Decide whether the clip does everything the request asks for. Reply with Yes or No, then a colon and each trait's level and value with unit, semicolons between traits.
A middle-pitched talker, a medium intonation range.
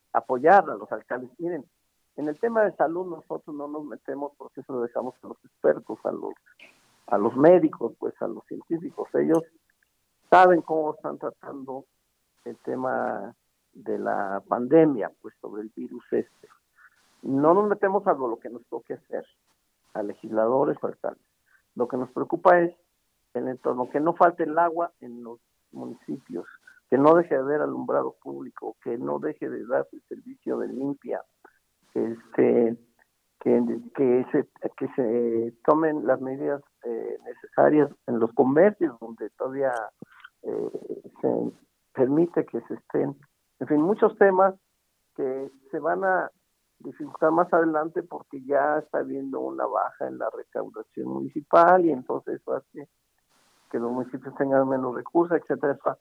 No: medium, 155 Hz; wide, 6.0 semitones